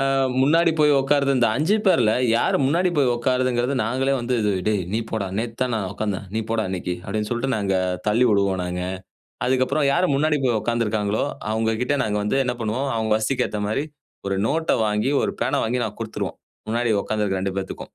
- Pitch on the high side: No, low, 115 Hz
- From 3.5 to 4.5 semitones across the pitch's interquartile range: Yes, average, 4.2 semitones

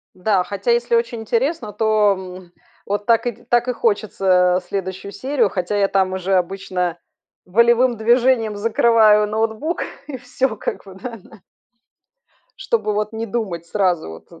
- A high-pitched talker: Yes, high, 210 Hz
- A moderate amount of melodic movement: Yes, average, 3.7 semitones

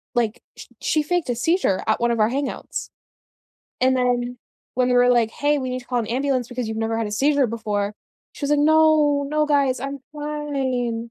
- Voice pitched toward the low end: No, very high, 255 Hz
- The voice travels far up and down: No, average, 3.6 semitones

